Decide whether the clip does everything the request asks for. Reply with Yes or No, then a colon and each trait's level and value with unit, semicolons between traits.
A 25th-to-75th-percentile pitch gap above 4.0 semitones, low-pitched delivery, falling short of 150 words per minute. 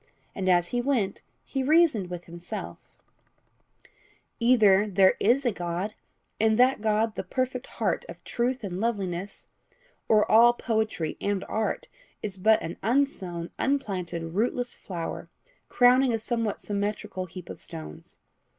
No: average, 4.8 semitones; high, 215 Hz; slow, 135 wpm